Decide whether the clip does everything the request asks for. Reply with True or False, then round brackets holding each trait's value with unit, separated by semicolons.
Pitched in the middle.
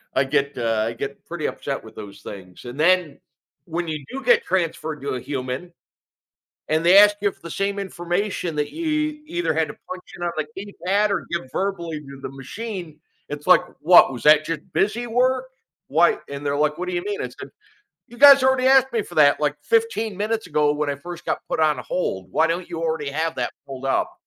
True (165 Hz)